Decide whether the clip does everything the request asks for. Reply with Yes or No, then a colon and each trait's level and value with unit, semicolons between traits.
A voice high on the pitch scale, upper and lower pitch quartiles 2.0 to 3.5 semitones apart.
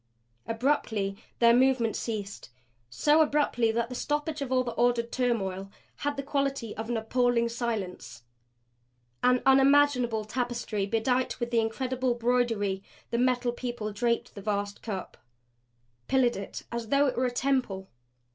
Yes: high, 240 Hz; average, 2.7 semitones